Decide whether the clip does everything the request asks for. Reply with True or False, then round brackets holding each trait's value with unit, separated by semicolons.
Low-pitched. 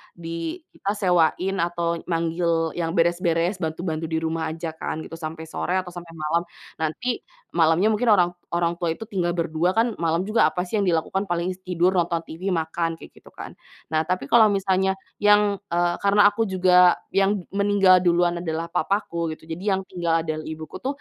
False (175 Hz)